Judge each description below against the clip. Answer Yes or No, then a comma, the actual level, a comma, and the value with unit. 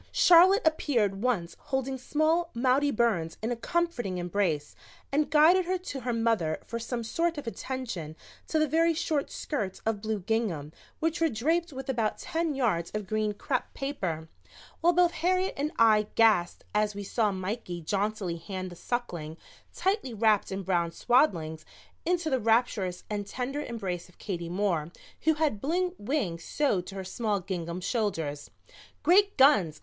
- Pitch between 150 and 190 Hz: No, high, 225 Hz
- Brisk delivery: No, average, 165 wpm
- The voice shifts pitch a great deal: Yes, wide, 7.9 semitones